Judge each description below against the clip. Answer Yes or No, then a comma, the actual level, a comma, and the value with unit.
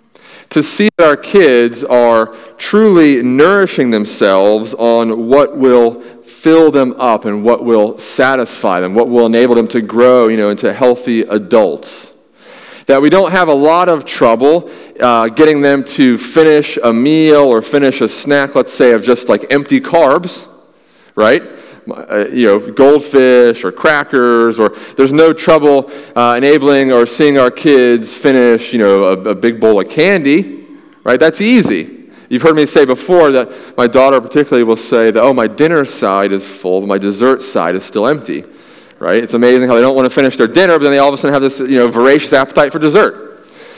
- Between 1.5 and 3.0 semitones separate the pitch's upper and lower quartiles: No, average, 3.9 semitones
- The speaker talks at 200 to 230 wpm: No, average, 185 wpm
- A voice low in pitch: Yes, low, 125 Hz